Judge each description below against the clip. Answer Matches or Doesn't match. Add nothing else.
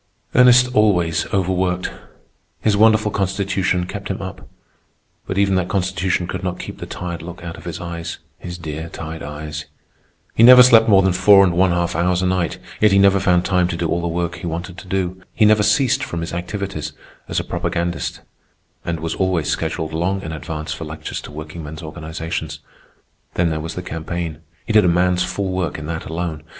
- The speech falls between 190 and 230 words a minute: Matches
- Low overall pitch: Matches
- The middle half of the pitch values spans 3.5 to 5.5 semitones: Doesn't match